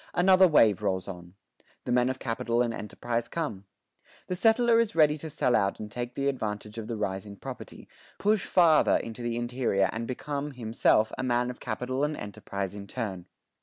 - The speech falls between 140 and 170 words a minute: No, average, 190 wpm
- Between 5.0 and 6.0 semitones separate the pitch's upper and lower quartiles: Yes, wide, 5.4 semitones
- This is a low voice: Yes, low, 120 Hz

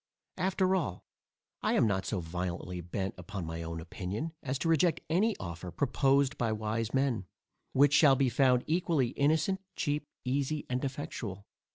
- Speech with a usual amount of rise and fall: No, wide, 7.5 semitones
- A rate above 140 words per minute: Yes, average, 160 wpm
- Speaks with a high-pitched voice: No, low, 130 Hz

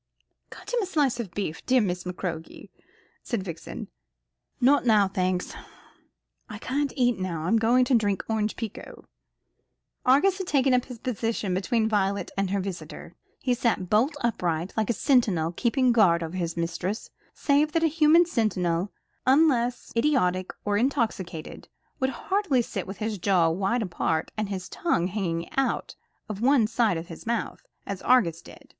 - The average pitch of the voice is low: No, high, 215 Hz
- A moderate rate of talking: Yes, average, 160 wpm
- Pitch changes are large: Yes, wide, 5.7 semitones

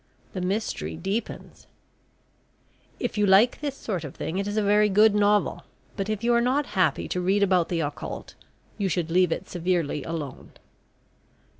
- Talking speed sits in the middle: Yes, average, 170 wpm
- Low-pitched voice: No, high, 195 Hz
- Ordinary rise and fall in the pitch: Yes, average, 3.3 semitones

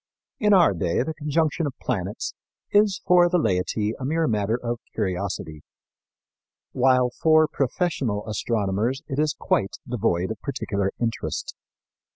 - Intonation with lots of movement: Yes, wide, 7.2 semitones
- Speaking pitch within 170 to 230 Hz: No, low, 125 Hz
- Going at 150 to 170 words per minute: No, slow, 135 wpm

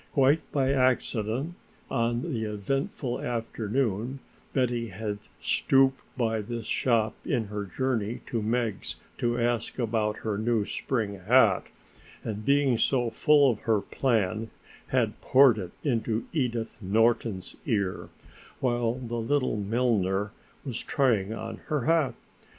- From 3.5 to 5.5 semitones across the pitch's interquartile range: No, average, 3.1 semitones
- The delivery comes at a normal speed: No, slow, 130 wpm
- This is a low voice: Yes, low, 115 Hz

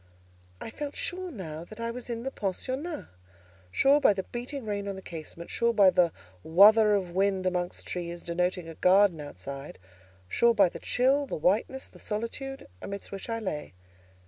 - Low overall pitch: No, high, 200 Hz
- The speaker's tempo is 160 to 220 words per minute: Yes, average, 170 wpm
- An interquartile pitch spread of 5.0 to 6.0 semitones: Yes, wide, 5.4 semitones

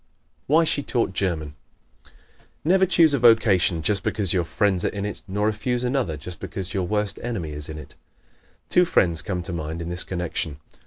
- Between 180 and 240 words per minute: Yes, average, 195 wpm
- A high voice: No, very low, 95 Hz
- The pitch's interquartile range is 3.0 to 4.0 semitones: No, wide, 5.5 semitones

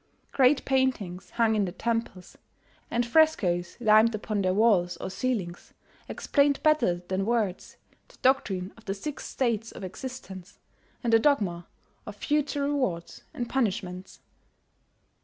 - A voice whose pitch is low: No, high, 220 Hz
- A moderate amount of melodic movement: No, wide, 5.8 semitones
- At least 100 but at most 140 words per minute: Yes, slow, 135 wpm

